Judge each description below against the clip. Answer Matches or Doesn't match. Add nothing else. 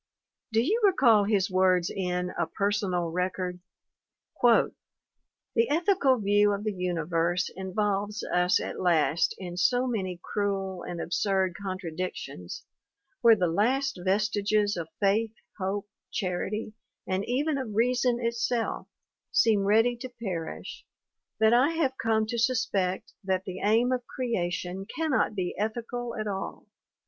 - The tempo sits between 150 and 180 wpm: Doesn't match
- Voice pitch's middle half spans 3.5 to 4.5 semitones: Matches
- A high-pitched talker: Matches